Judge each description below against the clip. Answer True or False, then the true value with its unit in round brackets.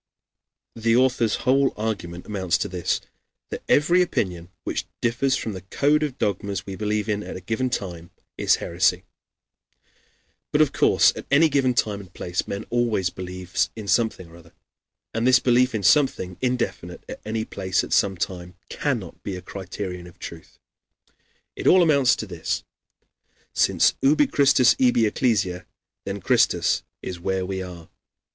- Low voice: True (105 Hz)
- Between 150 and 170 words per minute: True (165 wpm)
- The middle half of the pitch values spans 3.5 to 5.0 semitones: False (5.4 semitones)